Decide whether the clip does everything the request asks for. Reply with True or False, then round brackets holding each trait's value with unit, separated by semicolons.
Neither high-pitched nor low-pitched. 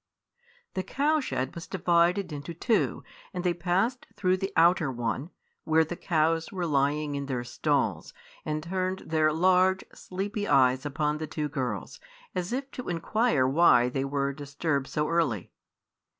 True (165 Hz)